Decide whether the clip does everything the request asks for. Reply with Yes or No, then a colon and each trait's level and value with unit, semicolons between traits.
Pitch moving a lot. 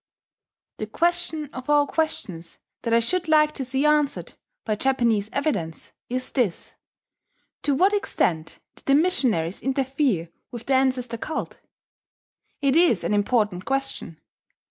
Yes: wide, 5.7 semitones